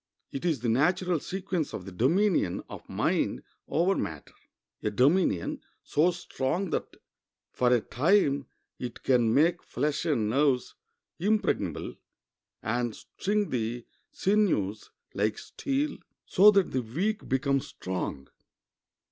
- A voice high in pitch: No, medium, 140 Hz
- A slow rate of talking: Yes, slow, 120 wpm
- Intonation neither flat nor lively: No, wide, 7.5 semitones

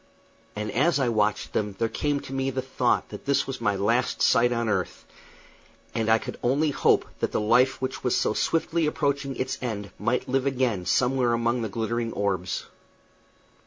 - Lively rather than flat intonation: No, average, 3.5 semitones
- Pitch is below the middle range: Yes, low, 120 Hz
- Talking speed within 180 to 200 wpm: Yes, average, 185 wpm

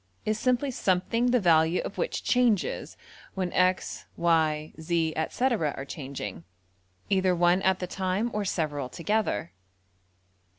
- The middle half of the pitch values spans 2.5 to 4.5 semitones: No, average, 5.0 semitones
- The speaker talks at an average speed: No, slow, 120 wpm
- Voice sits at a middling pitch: Yes, medium, 180 Hz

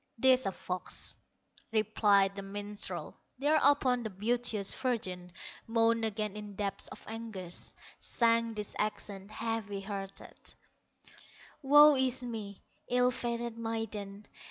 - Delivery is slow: Yes, slow, 110 wpm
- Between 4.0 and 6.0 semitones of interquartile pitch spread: No, average, 3.0 semitones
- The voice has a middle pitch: No, high, 220 Hz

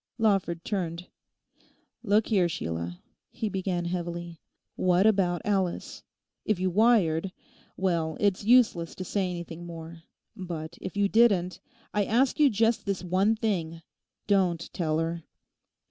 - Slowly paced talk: Yes, slow, 130 wpm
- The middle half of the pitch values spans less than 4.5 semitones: Yes, average, 3.4 semitones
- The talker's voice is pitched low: No, medium, 185 Hz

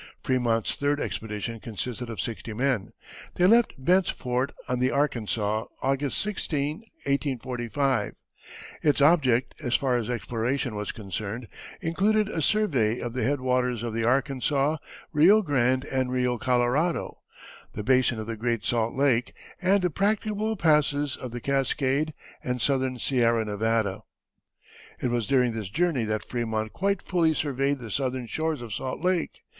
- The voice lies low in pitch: Yes, low, 130 Hz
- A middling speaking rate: Yes, average, 150 wpm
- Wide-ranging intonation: No, average, 4.0 semitones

